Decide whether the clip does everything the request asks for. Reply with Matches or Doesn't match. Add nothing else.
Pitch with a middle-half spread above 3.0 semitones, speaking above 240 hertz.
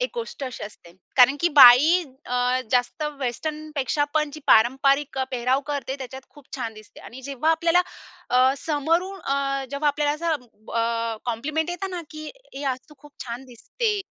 Matches